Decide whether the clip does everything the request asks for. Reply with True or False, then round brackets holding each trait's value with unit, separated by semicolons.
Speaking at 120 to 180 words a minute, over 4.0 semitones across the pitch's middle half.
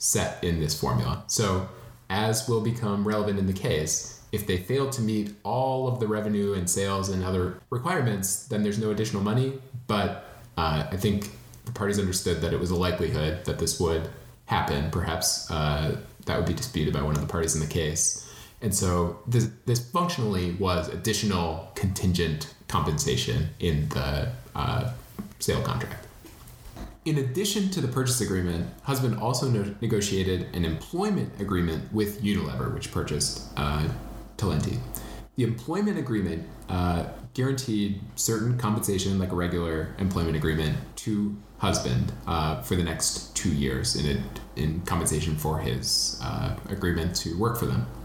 True (155 wpm; 5.1 semitones)